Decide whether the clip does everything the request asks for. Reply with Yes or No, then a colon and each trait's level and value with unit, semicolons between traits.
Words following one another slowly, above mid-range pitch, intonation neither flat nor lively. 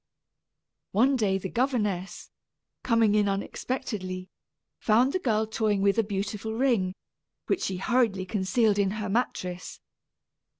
Yes: slow, 125 wpm; high, 210 Hz; average, 3.3 semitones